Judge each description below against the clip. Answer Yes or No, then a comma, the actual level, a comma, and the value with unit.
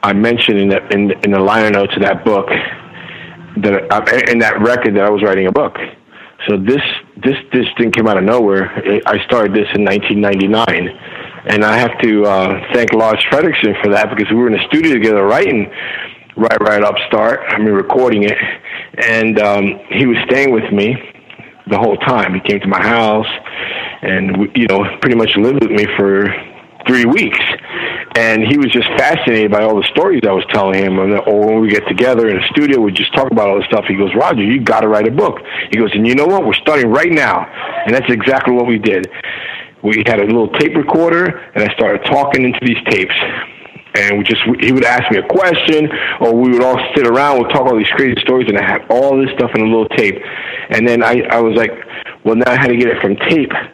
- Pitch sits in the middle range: No, low, 110 Hz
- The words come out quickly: Yes, fast, 225 wpm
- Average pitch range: Yes, average, 3.1 semitones